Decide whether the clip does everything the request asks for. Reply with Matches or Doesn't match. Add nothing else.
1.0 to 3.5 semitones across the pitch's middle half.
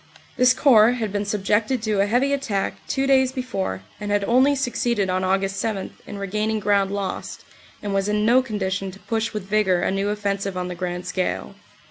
Matches